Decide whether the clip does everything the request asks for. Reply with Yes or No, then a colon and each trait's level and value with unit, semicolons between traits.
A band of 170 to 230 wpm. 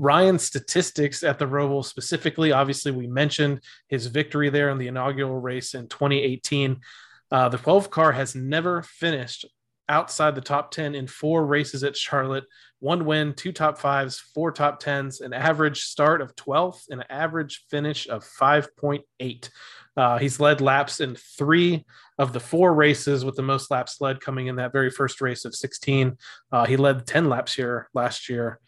Yes: average, 175 wpm